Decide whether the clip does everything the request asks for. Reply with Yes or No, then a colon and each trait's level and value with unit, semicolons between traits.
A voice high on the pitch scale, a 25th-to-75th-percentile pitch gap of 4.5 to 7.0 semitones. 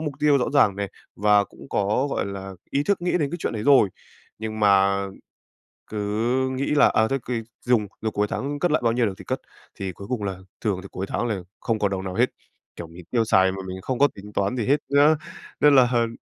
No: low, 110 Hz; average, 5.0 semitones